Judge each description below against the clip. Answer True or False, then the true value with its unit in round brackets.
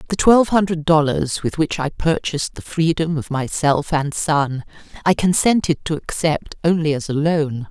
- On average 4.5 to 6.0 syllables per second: True (4.7 syllables/s)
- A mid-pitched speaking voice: True (160 Hz)